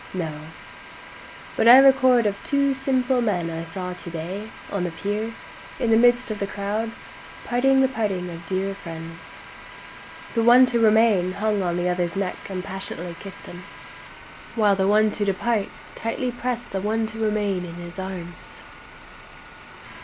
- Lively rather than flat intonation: No, average, 4.2 semitones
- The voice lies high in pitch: Yes, high, 200 Hz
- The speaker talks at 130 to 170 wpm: Yes, average, 155 wpm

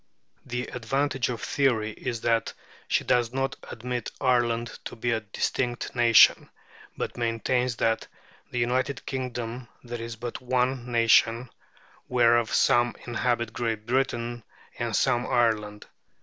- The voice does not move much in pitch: Yes, narrow, 1.4 semitones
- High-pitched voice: No, low, 120 Hz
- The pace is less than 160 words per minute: Yes, slow, 135 wpm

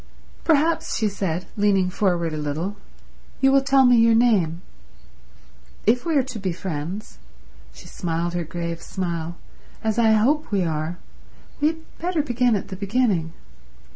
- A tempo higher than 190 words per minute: No, average, 145 wpm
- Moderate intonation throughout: No, wide, 6.4 semitones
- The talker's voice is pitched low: No, high, 200 Hz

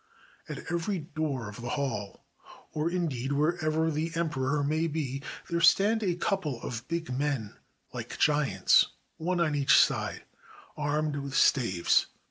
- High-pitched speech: No, medium, 150 Hz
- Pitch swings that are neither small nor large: Yes, average, 3.6 semitones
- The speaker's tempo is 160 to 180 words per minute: No, average, 140 wpm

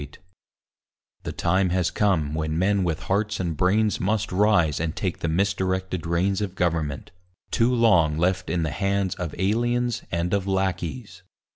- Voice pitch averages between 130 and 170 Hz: No, very low, 95 Hz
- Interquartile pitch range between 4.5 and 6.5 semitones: No, average, 3.1 semitones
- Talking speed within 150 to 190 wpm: Yes, average, 160 wpm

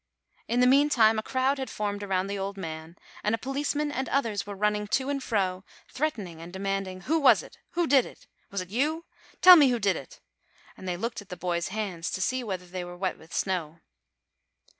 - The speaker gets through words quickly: Yes, fast, 215 wpm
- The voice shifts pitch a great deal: Yes, wide, 5.9 semitones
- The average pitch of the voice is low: No, high, 205 Hz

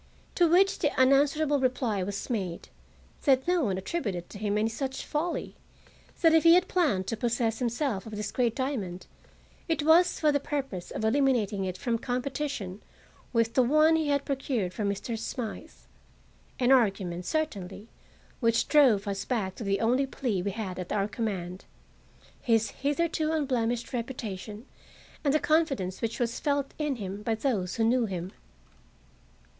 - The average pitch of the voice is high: Yes, high, 235 Hz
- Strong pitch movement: Yes, wide, 5.8 semitones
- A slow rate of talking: No, average, 160 wpm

